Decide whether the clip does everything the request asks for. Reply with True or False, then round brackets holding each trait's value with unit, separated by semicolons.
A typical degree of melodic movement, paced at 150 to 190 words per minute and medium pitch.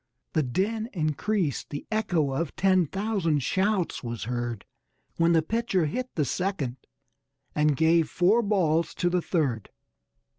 False (5.0 semitones; 140 wpm; 170 Hz)